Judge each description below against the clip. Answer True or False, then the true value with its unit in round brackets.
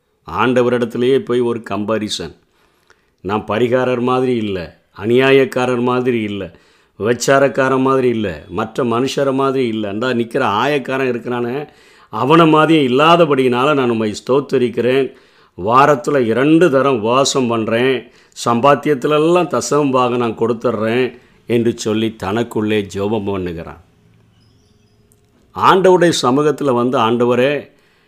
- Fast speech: False (100 wpm)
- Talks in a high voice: False (125 Hz)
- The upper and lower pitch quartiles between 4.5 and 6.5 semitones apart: False (3.3 semitones)